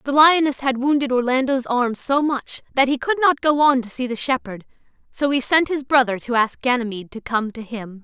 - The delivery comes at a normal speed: No, fast, 225 wpm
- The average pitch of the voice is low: No, very high, 255 Hz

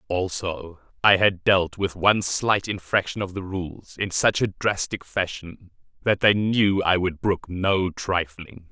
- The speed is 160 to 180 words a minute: Yes, average, 165 wpm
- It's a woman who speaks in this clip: No, male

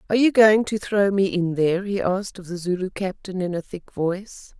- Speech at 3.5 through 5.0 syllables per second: No, 5.5 syllables/s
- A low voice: No, high, 190 Hz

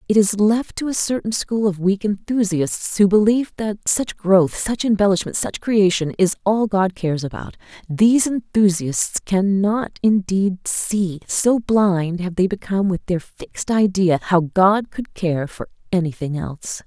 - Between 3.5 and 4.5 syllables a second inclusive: Yes, 4.4 syllables/s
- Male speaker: No, female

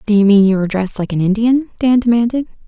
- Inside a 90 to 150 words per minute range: No, average, 200 wpm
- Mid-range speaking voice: No, high, 215 Hz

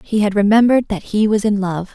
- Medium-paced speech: No, fast, 245 wpm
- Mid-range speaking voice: No, high, 210 Hz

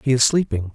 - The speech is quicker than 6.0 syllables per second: Yes, 6.3 syllables/s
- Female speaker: No, male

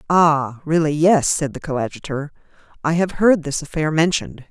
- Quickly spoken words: No, average, 160 wpm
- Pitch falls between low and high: Yes, medium, 155 Hz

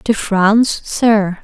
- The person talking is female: Yes, female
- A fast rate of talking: No, slow, 125 wpm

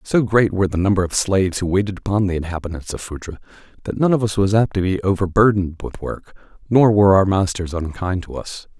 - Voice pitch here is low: Yes, very low, 95 Hz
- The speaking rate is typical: No, fast, 220 wpm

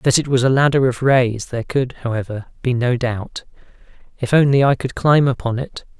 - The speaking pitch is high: No, low, 125 Hz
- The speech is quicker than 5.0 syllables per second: Yes, 5.2 syllables/s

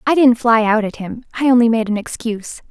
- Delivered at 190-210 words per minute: No, fast, 220 wpm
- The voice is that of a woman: Yes, female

